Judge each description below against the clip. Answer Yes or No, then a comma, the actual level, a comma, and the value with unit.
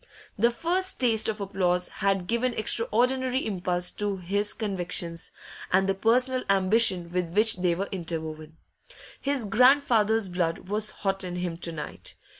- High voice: Yes, high, 195 Hz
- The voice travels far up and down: No, average, 4.3 semitones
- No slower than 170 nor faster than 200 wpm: No, average, 145 wpm